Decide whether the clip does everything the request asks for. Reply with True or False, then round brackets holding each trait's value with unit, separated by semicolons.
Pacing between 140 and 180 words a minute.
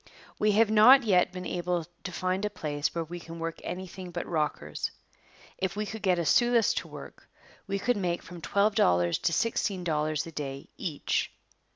False (190 wpm)